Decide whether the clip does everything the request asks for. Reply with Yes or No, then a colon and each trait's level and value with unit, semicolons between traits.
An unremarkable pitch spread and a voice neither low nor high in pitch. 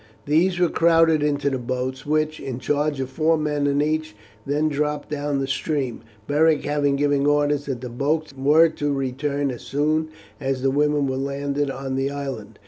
No: narrow, 1.9 semitones; medium, 145 Hz